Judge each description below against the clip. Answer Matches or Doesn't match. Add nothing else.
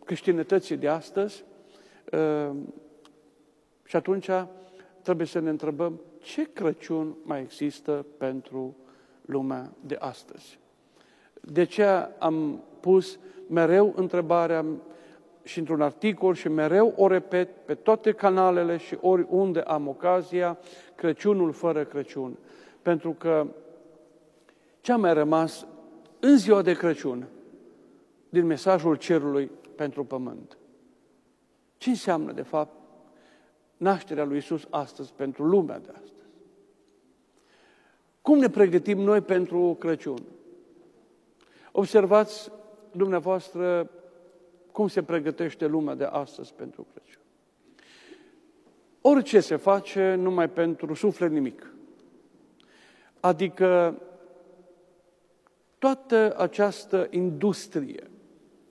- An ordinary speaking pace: Doesn't match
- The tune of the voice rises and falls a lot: Doesn't match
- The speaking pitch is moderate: Matches